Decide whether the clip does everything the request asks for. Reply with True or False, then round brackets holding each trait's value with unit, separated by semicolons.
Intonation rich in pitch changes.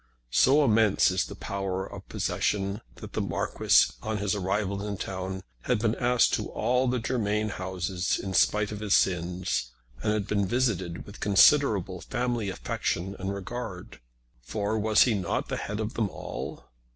False (2.7 semitones)